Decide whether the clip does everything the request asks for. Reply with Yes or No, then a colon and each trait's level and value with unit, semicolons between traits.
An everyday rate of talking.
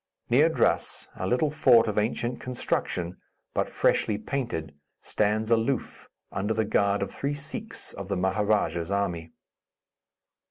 No: slow, 130 wpm